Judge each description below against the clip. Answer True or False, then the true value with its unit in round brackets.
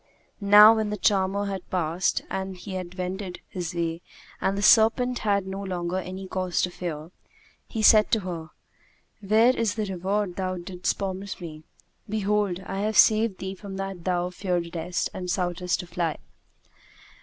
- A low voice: False (190 Hz)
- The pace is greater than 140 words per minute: True (160 wpm)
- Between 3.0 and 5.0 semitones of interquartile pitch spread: False (2.4 semitones)